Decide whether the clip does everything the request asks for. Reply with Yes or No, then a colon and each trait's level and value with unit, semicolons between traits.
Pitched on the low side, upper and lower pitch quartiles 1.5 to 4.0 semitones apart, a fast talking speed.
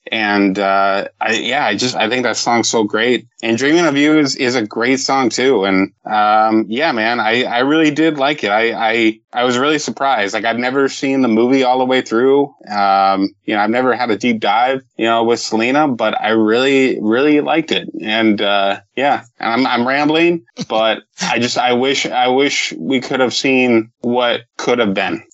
Yes: low, 120 Hz; average, 3.5 semitones; fast, 210 wpm